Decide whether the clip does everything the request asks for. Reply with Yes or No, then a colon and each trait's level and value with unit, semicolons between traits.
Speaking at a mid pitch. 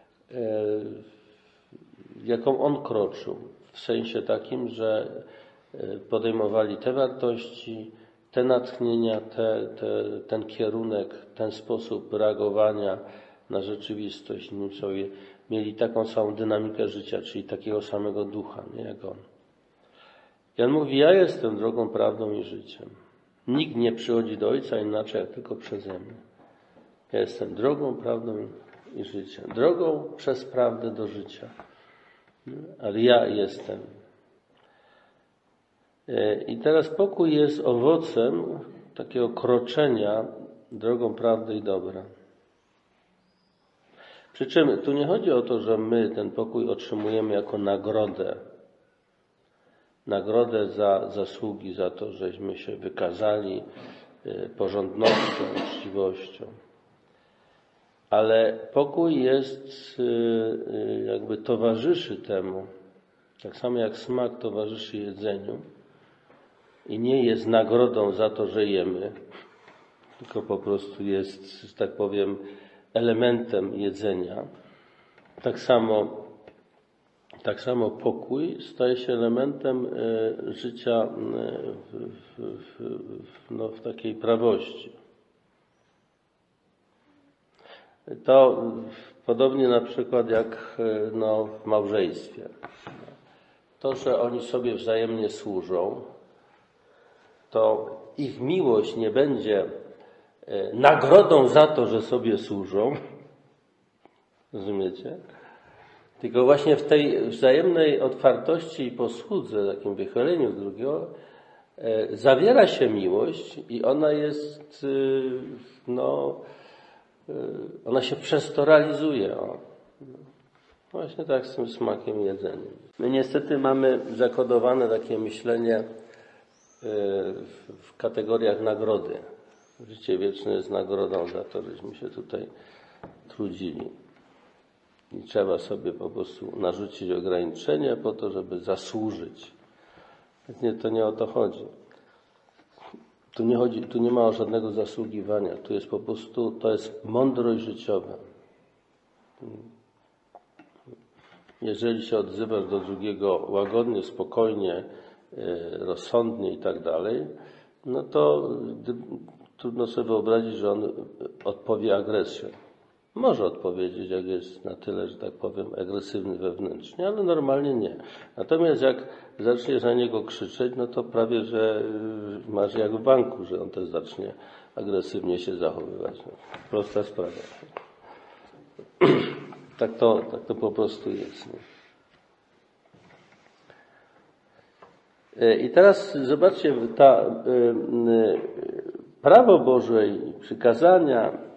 No: low, 120 Hz